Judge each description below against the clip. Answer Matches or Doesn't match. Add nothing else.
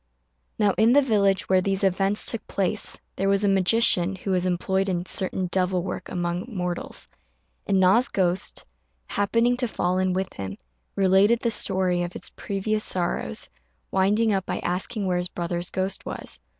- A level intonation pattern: Matches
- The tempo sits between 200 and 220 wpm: Doesn't match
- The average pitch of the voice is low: Doesn't match